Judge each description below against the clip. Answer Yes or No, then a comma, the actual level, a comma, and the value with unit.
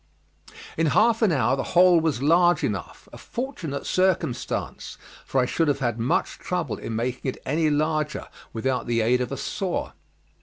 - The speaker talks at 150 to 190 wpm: Yes, average, 175 wpm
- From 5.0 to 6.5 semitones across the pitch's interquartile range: Yes, wide, 5.6 semitones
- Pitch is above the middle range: No, medium, 150 Hz